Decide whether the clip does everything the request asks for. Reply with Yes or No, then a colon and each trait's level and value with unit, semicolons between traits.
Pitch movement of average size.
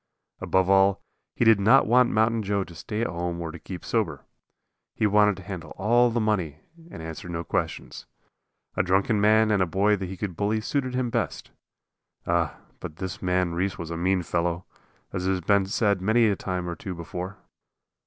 Yes: average, 3.4 semitones